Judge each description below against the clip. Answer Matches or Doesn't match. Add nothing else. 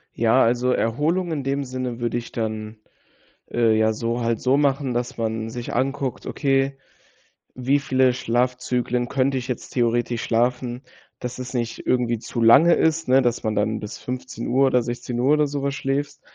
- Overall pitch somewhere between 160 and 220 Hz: Doesn't match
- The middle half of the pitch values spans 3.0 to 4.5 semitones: Doesn't match